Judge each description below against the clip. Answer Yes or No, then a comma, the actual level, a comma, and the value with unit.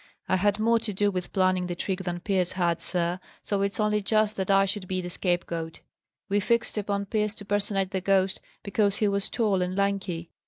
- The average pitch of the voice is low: No, high, 195 Hz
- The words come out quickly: Yes, fast, 210 wpm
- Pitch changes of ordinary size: No, narrow, 2.0 semitones